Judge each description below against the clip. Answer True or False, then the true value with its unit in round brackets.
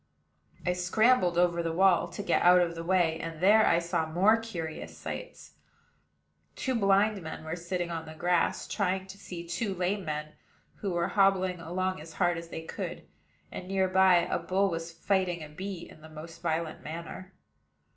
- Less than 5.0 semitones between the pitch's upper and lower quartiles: True (2.4 semitones)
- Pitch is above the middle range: False (175 Hz)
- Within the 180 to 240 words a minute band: True (185 wpm)